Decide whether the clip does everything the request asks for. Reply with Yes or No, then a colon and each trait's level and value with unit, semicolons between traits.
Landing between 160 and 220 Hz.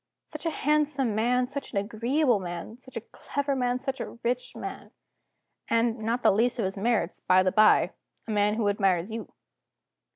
No: high, 230 Hz